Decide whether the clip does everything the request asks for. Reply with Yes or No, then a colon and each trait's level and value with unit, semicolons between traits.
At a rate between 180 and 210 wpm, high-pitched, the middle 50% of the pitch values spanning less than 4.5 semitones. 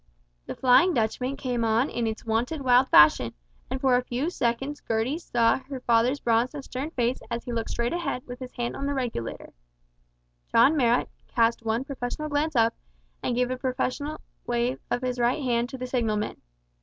Yes: average, 190 wpm; very high, 250 Hz; narrow, 2.4 semitones